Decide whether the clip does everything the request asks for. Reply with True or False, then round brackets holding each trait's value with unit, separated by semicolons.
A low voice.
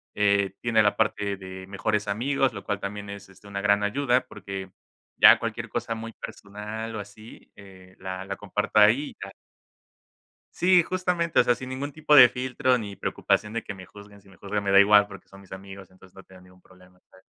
True (100 Hz)